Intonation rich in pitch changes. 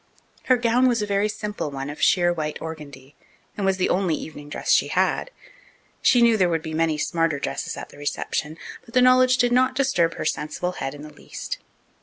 Yes: wide, 7.4 semitones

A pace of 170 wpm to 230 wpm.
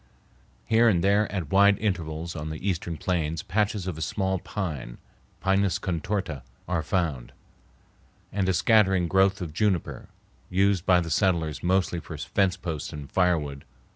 No: average, 150 wpm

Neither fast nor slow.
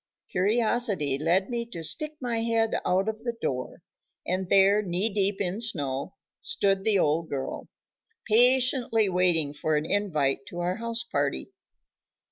Yes: average, 145 wpm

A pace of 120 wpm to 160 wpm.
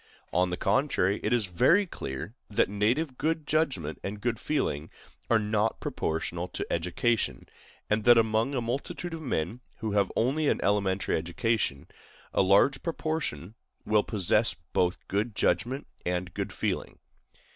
Yes: average, 145 wpm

